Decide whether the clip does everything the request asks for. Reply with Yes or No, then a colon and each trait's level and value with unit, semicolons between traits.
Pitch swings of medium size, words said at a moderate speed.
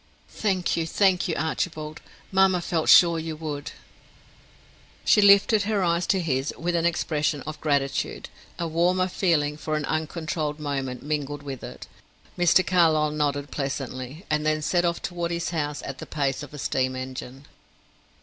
Yes: average, 3.1 semitones; average, 160 wpm